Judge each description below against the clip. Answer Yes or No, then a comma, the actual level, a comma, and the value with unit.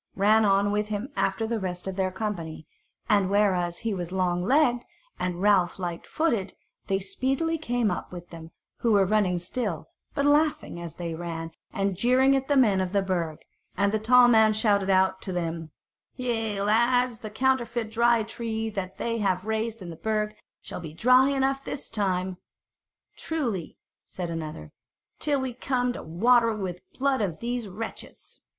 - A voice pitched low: No, high, 210 Hz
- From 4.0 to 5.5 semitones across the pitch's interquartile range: Yes, average, 4.6 semitones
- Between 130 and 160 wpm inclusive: No, average, 175 wpm